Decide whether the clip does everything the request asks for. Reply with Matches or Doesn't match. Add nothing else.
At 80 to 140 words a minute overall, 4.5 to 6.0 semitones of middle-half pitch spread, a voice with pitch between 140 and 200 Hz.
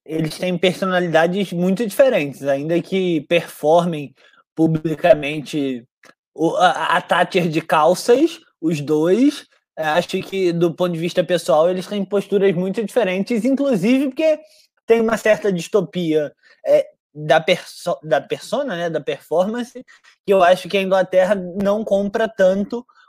Matches